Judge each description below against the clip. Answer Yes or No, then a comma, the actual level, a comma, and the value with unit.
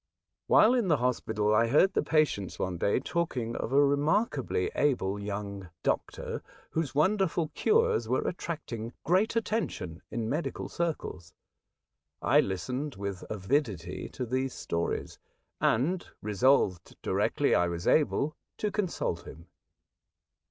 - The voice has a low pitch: Yes, low, 130 Hz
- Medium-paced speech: No, slow, 125 wpm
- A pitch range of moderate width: No, wide, 8.3 semitones